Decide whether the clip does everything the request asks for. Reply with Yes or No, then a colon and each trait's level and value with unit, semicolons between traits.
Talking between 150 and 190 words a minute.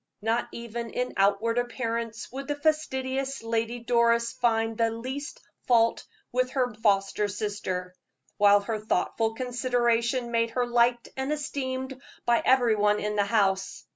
No: average, 140 wpm